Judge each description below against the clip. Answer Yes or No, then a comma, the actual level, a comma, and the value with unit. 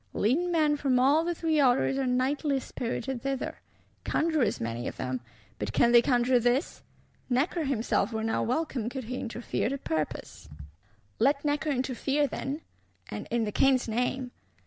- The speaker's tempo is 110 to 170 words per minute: Yes, average, 160 wpm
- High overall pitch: Yes, very high, 255 Hz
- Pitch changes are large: No, average, 3.3 semitones